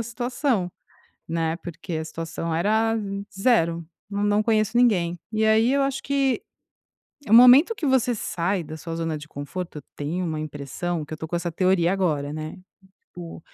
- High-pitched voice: No, medium, 180 Hz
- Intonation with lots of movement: Yes, wide, 5.7 semitones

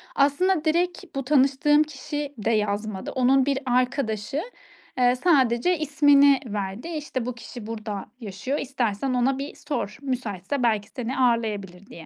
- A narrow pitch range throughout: No, average, 4.6 semitones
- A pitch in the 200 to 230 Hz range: No, very high, 255 Hz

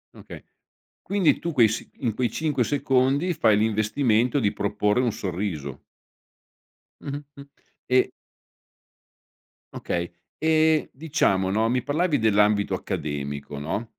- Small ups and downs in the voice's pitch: No, wide, 6.0 semitones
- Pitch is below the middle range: Yes, low, 115 Hz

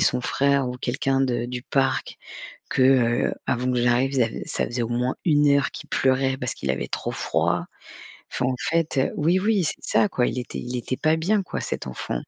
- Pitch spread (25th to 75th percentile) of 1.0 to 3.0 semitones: Yes, narrow, 2.5 semitones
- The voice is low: Yes, low, 130 Hz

